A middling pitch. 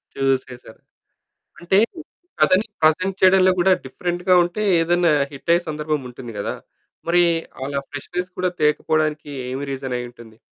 Yes: medium, 155 Hz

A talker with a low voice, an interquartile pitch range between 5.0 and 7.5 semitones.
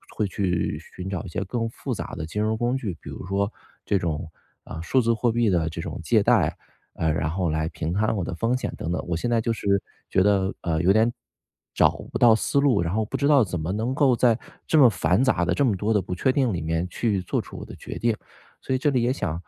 Yes: low, 105 Hz; wide, 5.4 semitones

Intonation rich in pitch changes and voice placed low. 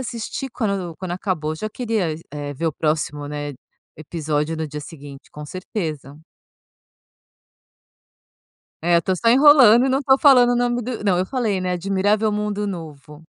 No: wide, 6.5 semitones; medium, 185 Hz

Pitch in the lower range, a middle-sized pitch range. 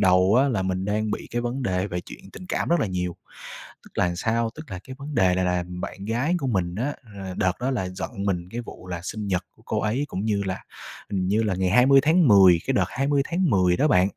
No: low, 100 Hz; wide, 5.7 semitones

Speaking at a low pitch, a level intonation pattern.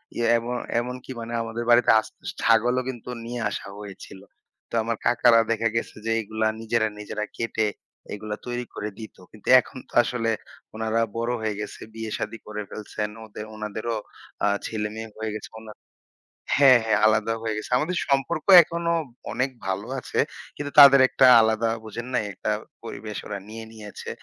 Yes: low, 115 Hz; narrow, 2.0 semitones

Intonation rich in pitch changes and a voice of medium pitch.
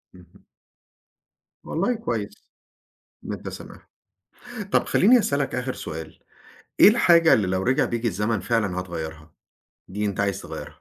No: wide, 7.0 semitones; low, 105 Hz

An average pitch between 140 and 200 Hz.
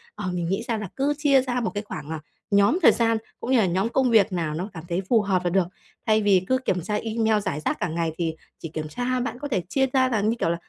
No: high, 210 Hz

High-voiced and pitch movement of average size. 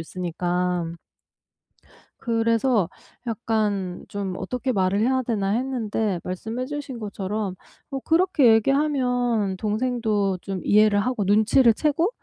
Yes: high, 220 Hz; average, 4.4 semitones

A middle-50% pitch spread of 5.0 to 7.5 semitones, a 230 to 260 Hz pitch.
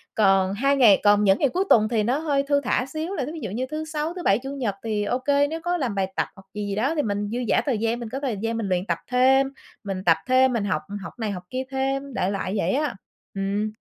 Yes: average, 5.3 semitones; high, 235 Hz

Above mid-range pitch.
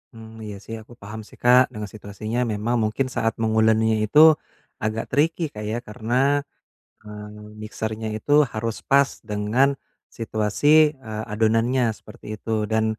No: low, 110 Hz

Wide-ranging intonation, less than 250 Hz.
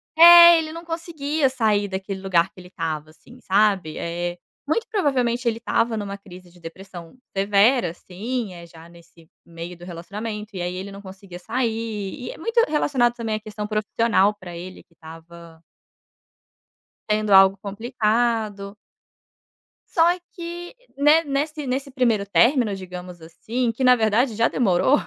Yes: wide, 5.7 semitones; high, 210 Hz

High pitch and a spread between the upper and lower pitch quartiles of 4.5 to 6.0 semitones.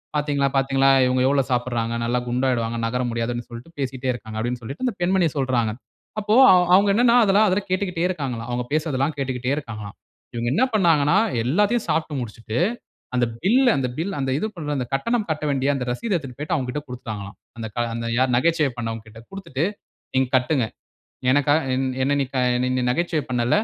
No: low, 135 Hz; average, 4.9 semitones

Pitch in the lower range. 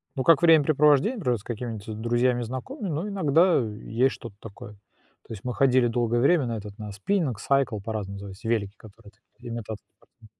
Yes: low, 120 Hz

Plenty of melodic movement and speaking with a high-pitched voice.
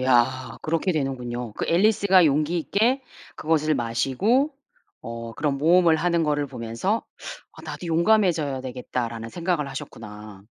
No: wide, 6.0 semitones; medium, 150 Hz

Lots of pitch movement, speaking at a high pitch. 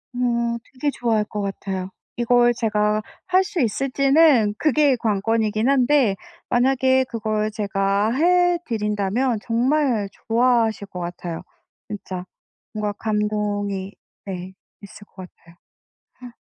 No: average, 3.8 semitones; high, 225 Hz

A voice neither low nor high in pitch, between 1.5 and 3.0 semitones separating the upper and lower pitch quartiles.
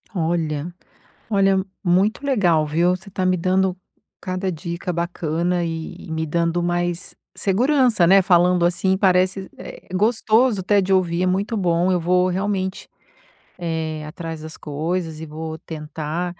Yes: medium, 180 Hz; narrow, 2.5 semitones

